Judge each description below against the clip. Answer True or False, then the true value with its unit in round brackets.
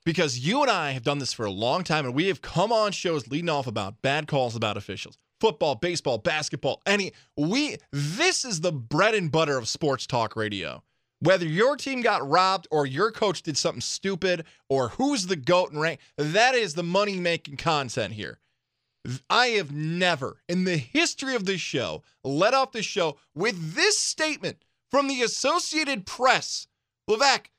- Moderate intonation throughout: False (7.2 semitones)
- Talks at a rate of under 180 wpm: False (185 wpm)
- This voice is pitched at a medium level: True (170 Hz)